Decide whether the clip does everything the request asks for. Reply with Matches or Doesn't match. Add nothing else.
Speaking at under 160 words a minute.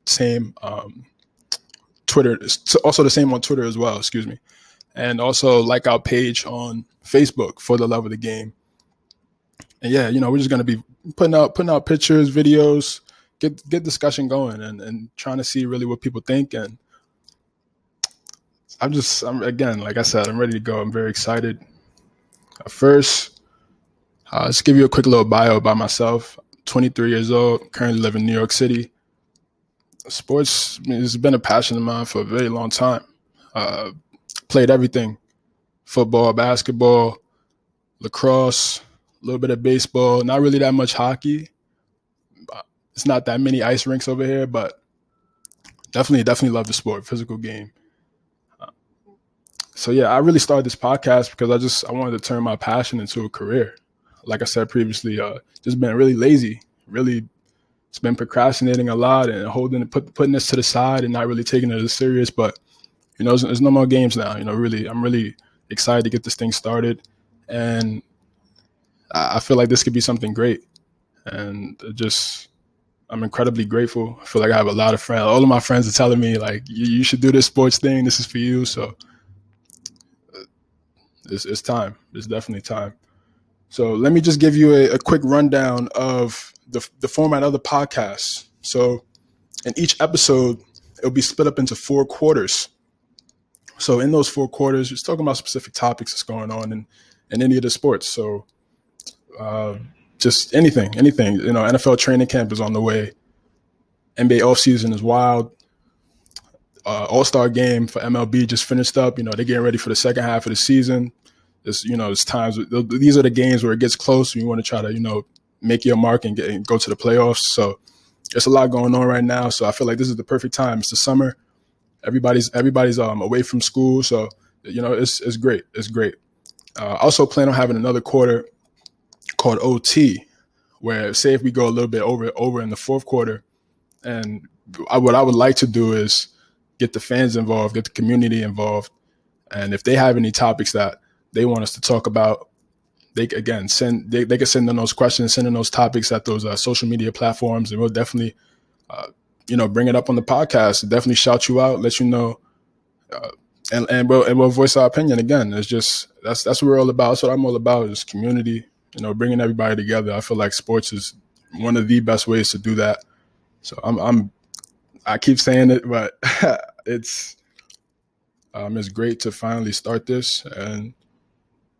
Doesn't match